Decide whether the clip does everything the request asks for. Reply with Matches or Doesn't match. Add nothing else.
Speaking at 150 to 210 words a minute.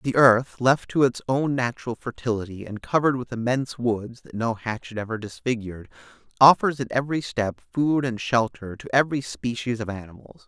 Matches